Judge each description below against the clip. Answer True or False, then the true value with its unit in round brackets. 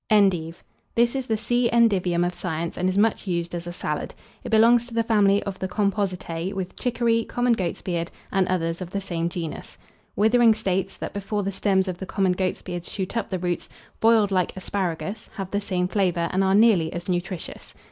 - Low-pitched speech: False (190 Hz)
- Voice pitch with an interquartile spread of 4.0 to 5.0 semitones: False (3.3 semitones)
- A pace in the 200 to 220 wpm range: True (205 wpm)